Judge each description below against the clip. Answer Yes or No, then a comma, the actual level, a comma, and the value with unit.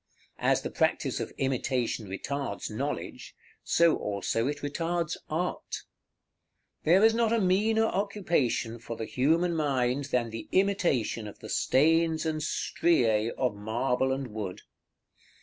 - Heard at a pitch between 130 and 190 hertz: Yes, medium, 140 Hz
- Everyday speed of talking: No, slow, 130 wpm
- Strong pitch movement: Yes, wide, 6.5 semitones